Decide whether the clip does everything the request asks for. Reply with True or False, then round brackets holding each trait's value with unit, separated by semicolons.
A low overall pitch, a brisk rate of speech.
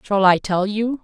False (205 Hz; 230 wpm)